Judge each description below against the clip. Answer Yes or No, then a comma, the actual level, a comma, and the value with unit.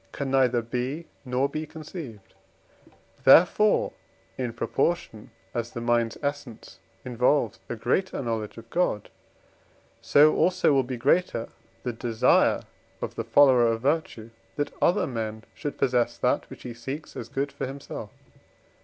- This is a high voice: No, low, 125 Hz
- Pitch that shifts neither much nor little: Yes, average, 3.7 semitones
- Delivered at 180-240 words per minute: No, average, 140 wpm